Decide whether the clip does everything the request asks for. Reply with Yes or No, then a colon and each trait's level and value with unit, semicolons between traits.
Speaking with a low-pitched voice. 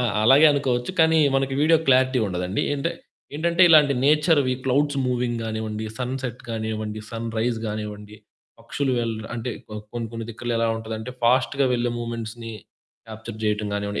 Yes: low, 120 Hz